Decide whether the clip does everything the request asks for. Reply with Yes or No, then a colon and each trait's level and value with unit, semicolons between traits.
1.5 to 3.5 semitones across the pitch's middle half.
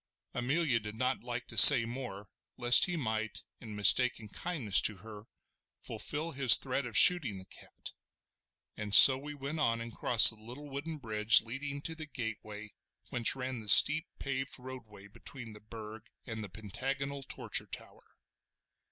No: average, 4.2 semitones